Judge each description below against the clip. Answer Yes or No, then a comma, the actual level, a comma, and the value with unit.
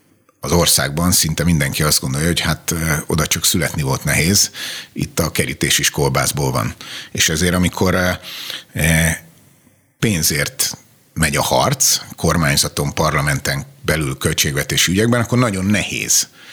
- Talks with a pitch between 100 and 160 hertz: No, very low, 90 Hz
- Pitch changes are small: No, average, 4.5 semitones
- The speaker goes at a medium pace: Yes, average, 125 wpm